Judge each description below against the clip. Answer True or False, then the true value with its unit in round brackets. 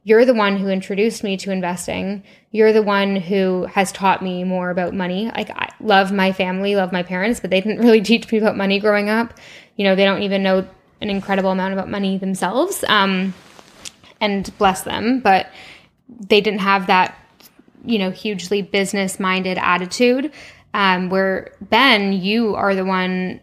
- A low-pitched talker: False (195 Hz)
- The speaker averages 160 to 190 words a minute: True (180 wpm)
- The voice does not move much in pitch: True (2.1 semitones)